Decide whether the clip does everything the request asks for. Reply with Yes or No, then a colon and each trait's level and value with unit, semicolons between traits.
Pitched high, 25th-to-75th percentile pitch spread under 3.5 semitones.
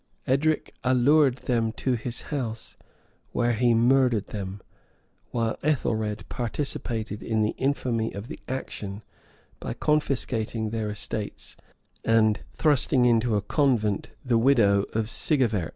No: low, 115 Hz; average, 3.1 semitones